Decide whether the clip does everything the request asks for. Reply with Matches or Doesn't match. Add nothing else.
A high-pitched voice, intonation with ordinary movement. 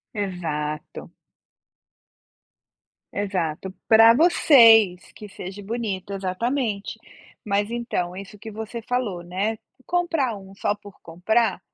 Matches